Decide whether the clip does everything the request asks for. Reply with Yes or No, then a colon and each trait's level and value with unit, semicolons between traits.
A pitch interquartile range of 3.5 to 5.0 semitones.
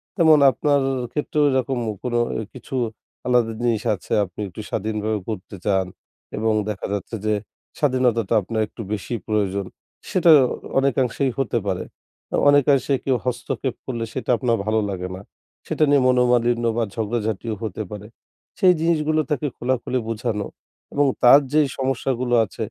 Yes: average, 3.8 semitones